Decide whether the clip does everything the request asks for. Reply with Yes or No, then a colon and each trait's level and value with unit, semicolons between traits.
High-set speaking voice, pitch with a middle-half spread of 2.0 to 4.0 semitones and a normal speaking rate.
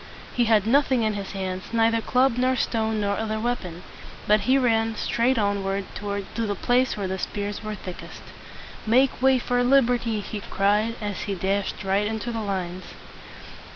Yes: high, 215 Hz; average, 3.0 semitones; average, 185 wpm